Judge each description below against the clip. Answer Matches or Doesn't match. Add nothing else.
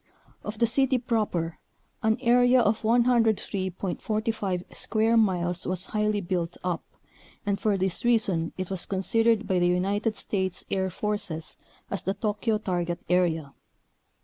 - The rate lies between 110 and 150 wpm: Matches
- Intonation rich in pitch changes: Doesn't match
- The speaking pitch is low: Doesn't match